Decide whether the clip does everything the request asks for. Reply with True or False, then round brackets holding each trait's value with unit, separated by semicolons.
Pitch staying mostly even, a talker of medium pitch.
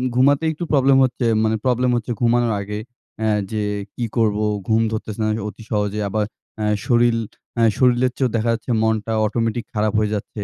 False (2.2 semitones; 115 Hz)